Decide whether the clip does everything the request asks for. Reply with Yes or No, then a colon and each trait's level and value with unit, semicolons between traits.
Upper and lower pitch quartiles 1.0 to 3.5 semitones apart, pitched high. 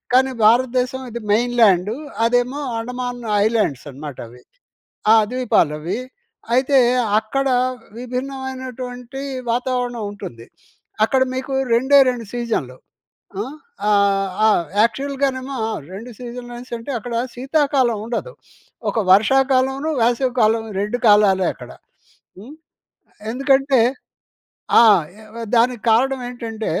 Yes: average, 3.0 semitones; high, 245 Hz